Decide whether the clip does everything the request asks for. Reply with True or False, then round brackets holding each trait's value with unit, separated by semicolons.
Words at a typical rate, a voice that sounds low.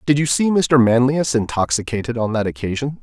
True (180 wpm; 125 Hz)